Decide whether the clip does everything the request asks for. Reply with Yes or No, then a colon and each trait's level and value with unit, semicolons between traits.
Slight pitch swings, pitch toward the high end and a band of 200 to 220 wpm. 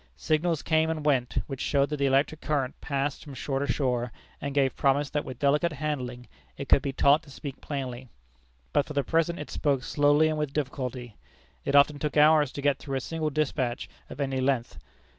No: narrow, 2.2 semitones; medium, 140 Hz; fast, 205 wpm